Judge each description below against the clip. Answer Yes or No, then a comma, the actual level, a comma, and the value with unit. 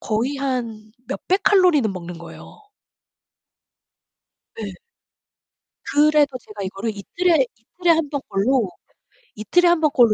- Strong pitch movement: Yes, wide, 6.9 semitones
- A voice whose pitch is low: No, very high, 265 Hz